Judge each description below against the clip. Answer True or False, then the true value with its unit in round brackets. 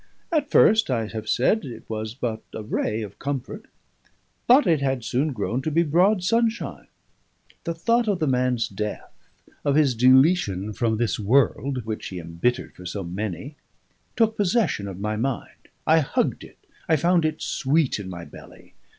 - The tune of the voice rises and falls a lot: True (7.3 semitones)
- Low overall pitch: True (130 Hz)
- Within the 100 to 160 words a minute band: False (170 wpm)